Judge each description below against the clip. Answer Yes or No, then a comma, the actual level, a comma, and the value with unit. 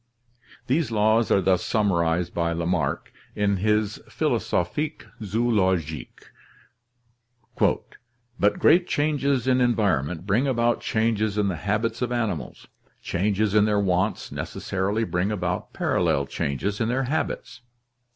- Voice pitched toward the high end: No, low, 105 Hz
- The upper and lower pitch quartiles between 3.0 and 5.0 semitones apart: Yes, average, 4.5 semitones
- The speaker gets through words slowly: Yes, slow, 120 wpm